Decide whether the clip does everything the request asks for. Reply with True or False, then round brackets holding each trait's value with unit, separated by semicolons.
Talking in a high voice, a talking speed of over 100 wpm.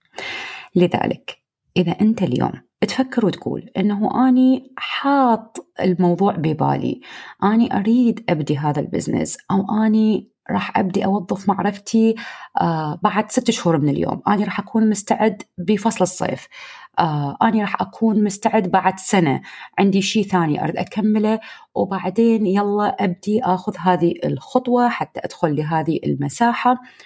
True (205 Hz; 120 wpm)